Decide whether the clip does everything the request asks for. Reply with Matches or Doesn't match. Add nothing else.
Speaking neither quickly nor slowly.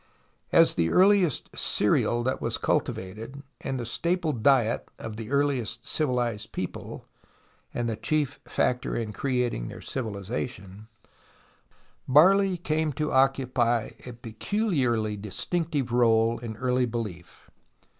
Doesn't match